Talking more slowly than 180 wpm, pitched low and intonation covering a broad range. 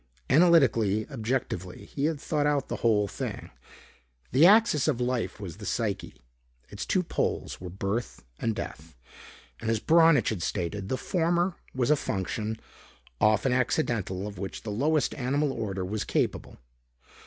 Yes: average, 150 wpm; low, 115 Hz; wide, 6.4 semitones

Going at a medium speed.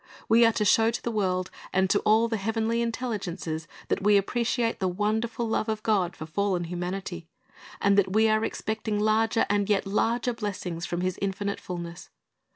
Yes: average, 180 wpm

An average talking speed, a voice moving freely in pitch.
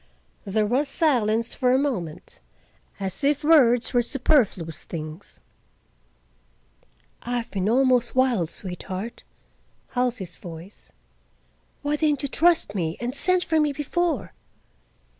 No: slow, 115 wpm; wide, 6.9 semitones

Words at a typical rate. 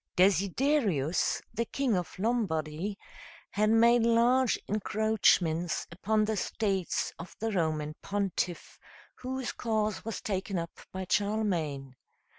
No: slow, 110 wpm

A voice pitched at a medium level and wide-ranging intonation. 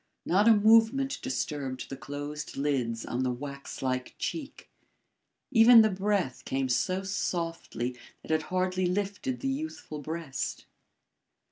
Yes: medium, 170 Hz; wide, 7.5 semitones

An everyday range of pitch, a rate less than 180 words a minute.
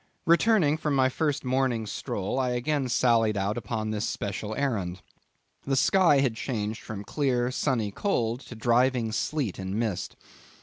Yes: average, 4.0 semitones; average, 150 wpm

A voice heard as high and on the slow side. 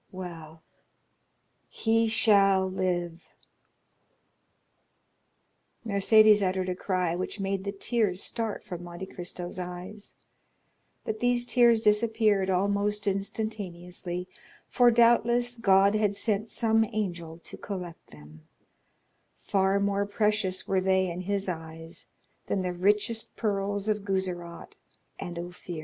Yes: high, 195 Hz; slow, 110 wpm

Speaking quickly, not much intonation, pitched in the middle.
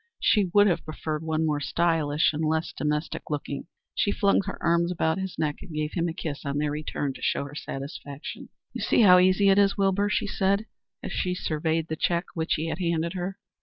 No: fast, 215 wpm; average, 3.6 semitones; medium, 165 Hz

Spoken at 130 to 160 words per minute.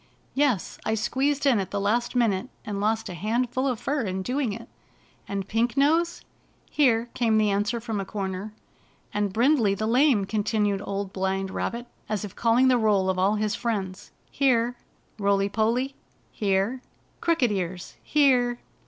No: average, 170 wpm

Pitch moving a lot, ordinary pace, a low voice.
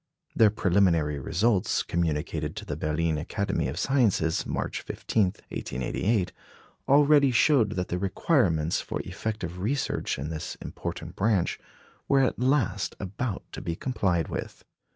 No: wide, 6.1 semitones; slow, 130 wpm; very low, 95 Hz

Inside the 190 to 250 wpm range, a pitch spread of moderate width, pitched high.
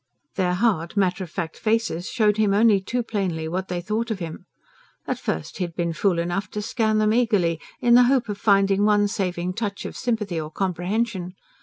Yes: average, 200 wpm; average, 3.6 semitones; high, 195 Hz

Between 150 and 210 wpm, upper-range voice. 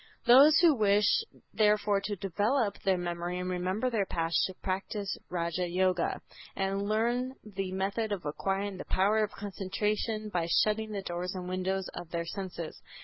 Yes: average, 160 wpm; high, 195 Hz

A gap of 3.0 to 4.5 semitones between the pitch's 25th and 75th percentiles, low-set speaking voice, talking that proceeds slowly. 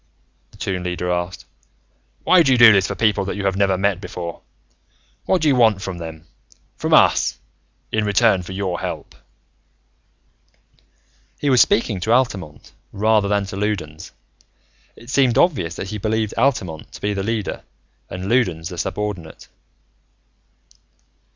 No: average, 3.7 semitones; low, 100 Hz; average, 150 wpm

